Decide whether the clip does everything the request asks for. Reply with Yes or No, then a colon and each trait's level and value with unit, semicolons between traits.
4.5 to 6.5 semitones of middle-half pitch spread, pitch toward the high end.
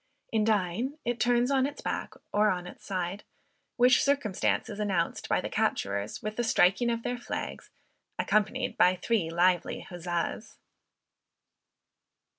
Yes: average, 5.1 semitones; high, 210 Hz